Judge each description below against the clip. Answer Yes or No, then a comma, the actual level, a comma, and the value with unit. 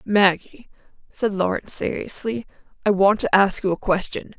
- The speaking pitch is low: No, high, 200 Hz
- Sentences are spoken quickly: No, average, 150 wpm